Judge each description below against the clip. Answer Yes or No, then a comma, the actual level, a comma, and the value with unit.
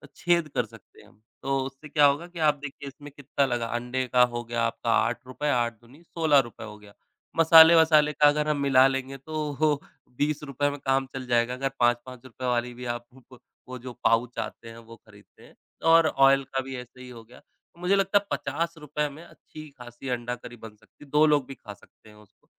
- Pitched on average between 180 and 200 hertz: No, low, 135 Hz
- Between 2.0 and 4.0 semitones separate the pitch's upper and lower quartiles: Yes, average, 3.7 semitones